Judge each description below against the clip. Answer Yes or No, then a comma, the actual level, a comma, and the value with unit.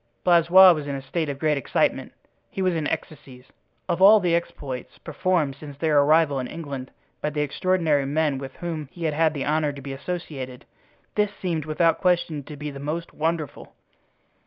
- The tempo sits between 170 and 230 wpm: Yes, average, 180 wpm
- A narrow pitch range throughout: No, average, 3.2 semitones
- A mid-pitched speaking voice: Yes, medium, 155 Hz